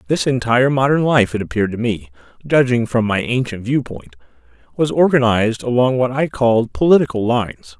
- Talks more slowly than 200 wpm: Yes, average, 160 wpm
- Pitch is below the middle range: Yes, low, 120 Hz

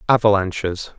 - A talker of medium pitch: No, low, 100 Hz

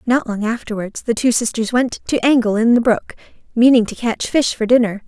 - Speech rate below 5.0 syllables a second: No, 5.3 syllables/s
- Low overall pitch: No, high, 230 Hz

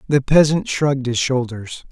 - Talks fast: No, average, 155 wpm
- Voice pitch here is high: No, low, 135 Hz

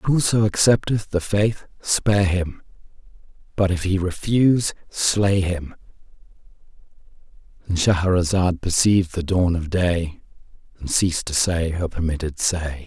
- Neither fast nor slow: No, slow, 115 wpm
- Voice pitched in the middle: No, very low, 90 Hz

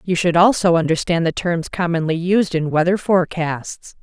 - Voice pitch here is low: No, medium, 170 Hz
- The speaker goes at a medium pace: Yes, average, 165 wpm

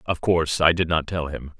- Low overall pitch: Yes, very low, 80 Hz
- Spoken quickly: Yes, fast, 265 wpm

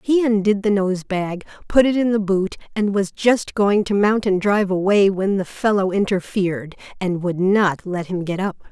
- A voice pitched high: Yes, high, 195 Hz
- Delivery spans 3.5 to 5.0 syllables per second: Yes, 4.7 syllables/s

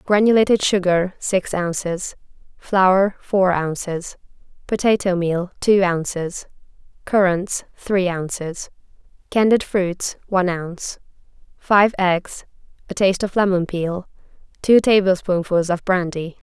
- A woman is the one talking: Yes, female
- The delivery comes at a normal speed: No, slow, 105 wpm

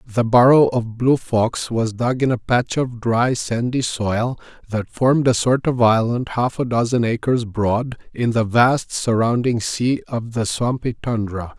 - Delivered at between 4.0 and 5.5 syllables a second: Yes, 4.1 syllables/s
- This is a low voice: Yes, low, 120 Hz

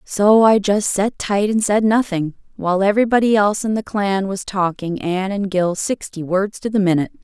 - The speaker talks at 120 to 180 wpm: No, average, 200 wpm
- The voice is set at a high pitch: Yes, high, 200 Hz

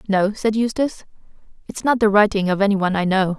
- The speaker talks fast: No, average, 195 wpm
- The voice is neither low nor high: No, high, 205 Hz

